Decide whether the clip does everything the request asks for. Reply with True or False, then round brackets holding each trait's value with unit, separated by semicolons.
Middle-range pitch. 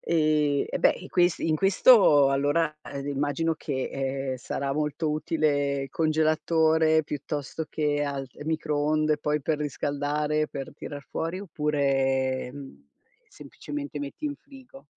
True (150 Hz)